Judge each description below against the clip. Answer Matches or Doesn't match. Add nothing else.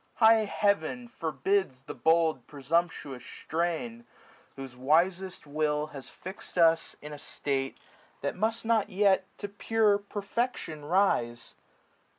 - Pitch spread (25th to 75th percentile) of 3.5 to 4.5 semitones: Doesn't match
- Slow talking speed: Matches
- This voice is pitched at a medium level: Matches